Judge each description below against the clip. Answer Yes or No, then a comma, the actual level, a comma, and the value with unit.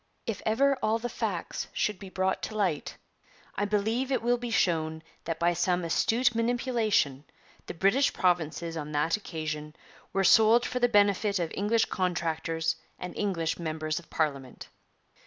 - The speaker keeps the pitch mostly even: No, wide, 5.5 semitones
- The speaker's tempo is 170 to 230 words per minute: No, average, 155 wpm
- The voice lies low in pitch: No, high, 190 Hz